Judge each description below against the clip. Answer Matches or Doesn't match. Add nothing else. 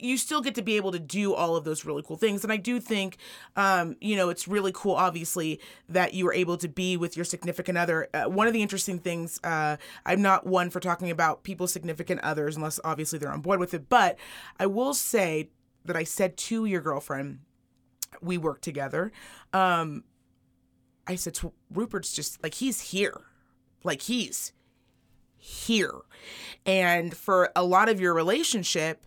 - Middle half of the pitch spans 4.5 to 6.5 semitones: Doesn't match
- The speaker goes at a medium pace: Matches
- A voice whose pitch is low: Doesn't match